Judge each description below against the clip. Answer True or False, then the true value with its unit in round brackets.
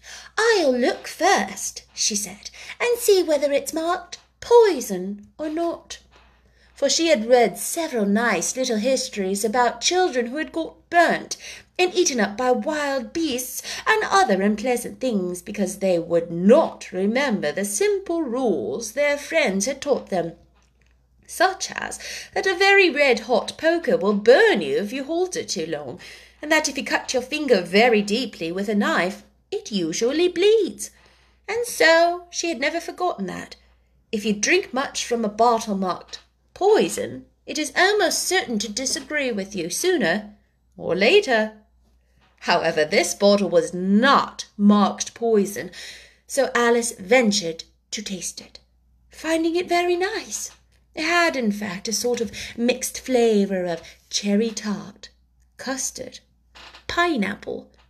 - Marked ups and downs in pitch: True (8.4 semitones)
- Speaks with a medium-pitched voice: False (245 Hz)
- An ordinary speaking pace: True (145 wpm)